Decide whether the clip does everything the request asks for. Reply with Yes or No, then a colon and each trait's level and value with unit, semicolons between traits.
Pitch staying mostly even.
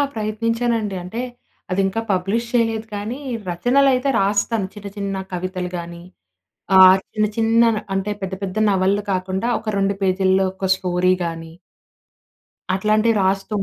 No: average, 3.0 semitones